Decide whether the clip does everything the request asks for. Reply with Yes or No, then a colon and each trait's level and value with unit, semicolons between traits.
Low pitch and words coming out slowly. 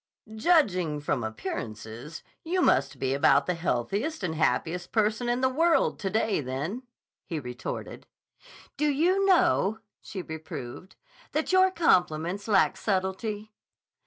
No: high, 190 Hz; slow, 130 wpm